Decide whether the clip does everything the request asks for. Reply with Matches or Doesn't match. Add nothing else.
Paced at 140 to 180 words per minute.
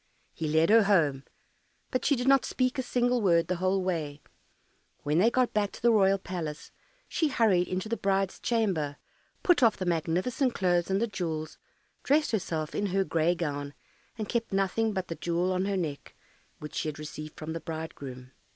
Doesn't match